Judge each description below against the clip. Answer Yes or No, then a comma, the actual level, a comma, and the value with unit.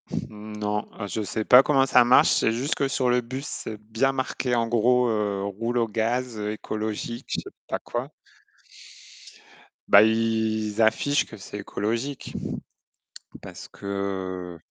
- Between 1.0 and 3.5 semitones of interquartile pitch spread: Yes, average, 2.8 semitones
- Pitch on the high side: No, low, 110 Hz